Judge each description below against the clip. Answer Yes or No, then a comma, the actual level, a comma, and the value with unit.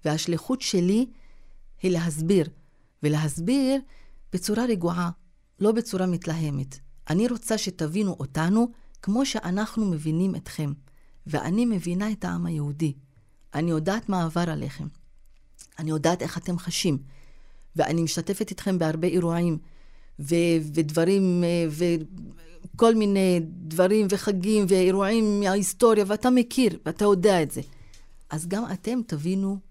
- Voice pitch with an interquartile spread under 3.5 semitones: No, average, 4.4 semitones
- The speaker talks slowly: No, average, 115 wpm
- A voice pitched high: No, medium, 175 Hz